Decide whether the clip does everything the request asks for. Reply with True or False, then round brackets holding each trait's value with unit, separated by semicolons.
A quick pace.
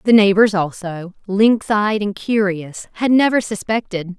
False (145 wpm)